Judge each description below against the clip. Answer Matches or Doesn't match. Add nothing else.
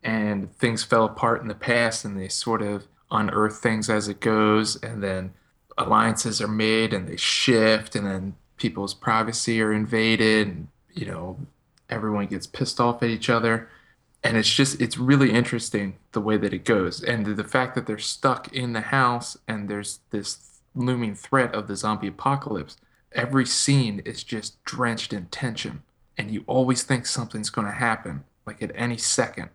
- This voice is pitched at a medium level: Doesn't match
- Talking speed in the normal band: Matches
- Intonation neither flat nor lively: Doesn't match